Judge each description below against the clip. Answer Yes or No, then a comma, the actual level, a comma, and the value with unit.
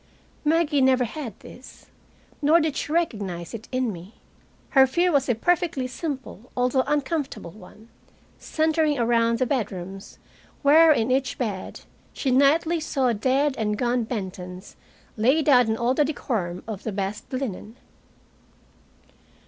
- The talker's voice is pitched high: Yes, very high, 255 Hz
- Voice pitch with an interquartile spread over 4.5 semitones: Yes, average, 5.1 semitones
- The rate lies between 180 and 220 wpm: No, average, 140 wpm